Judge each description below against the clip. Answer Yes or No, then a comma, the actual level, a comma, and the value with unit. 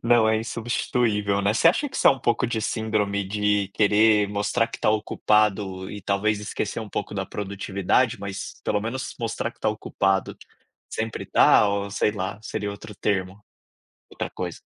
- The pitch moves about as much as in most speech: No, narrow, 1.7 semitones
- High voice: No, low, 105 Hz